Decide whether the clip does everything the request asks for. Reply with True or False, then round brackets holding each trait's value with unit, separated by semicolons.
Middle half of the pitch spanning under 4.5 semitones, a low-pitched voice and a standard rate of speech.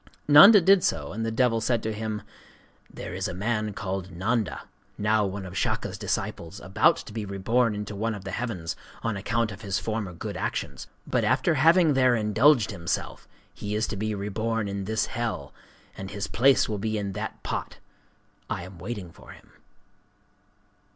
True (2.9 semitones; 105 Hz; 175 wpm)